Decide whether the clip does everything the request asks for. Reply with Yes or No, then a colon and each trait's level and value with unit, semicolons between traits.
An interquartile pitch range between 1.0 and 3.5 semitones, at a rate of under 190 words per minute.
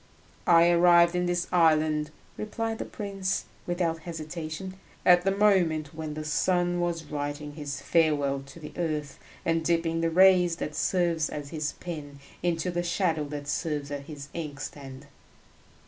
Yes: average, 2.7 semitones; average, 150 wpm